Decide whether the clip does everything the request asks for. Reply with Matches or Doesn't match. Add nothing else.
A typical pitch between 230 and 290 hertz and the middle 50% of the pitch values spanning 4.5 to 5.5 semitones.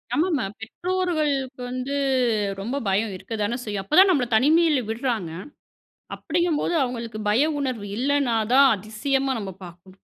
Matches